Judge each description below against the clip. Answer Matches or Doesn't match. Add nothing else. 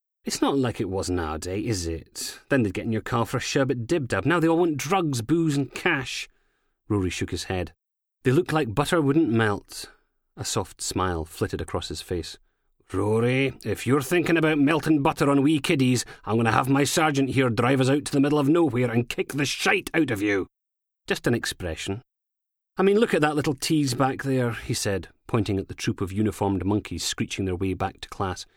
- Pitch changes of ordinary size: Doesn't match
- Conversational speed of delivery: Doesn't match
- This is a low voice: Matches